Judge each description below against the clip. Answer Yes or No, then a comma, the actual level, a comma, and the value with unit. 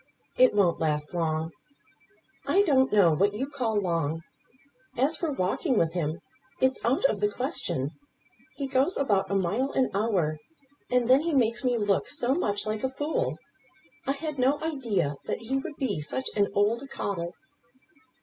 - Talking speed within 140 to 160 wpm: No, average, 170 wpm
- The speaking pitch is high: Yes, high, 230 Hz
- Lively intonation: Yes, wide, 6.6 semitones